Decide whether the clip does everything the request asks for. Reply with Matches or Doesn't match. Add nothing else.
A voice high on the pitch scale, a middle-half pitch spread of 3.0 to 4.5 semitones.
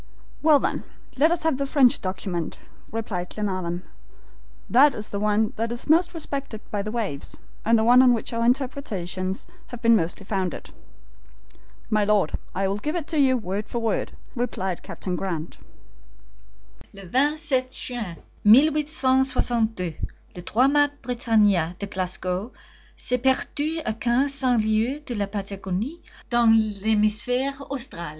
Doesn't match